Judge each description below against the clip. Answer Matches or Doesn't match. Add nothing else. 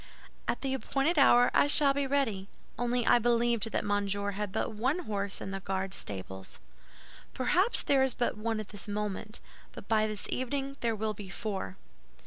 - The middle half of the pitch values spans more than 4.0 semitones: Matches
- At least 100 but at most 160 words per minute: Doesn't match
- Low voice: Doesn't match